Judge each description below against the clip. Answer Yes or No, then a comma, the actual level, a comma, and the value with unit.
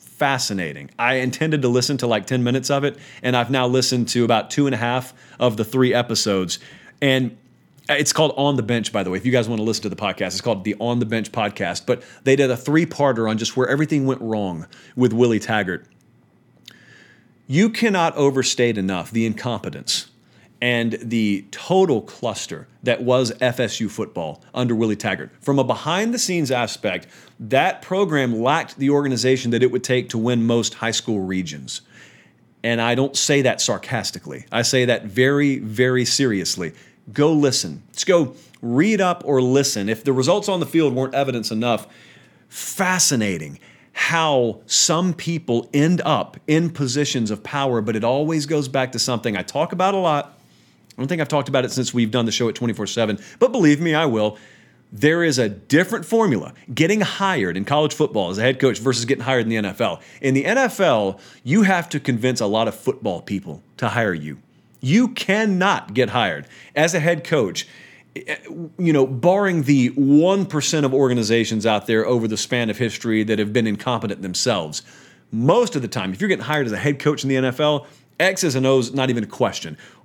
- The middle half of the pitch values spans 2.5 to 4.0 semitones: No, average, 4.4 semitones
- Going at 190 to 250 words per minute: Yes, average, 195 wpm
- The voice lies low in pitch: Yes, low, 130 Hz